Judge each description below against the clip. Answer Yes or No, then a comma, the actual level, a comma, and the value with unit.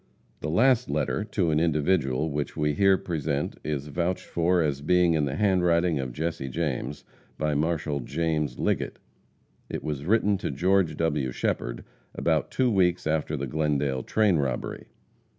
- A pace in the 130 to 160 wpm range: Yes, average, 155 wpm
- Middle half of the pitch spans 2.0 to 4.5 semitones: Yes, average, 3.7 semitones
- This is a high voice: No, very low, 80 Hz